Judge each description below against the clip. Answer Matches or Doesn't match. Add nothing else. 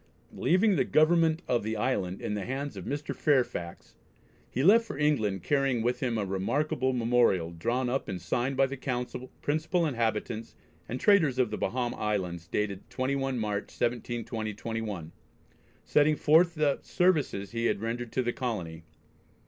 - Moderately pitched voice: Doesn't match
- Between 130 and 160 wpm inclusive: Matches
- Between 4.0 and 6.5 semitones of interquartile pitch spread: Matches